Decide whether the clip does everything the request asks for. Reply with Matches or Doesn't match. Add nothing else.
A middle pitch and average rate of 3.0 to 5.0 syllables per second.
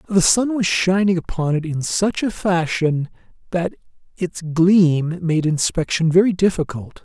Matches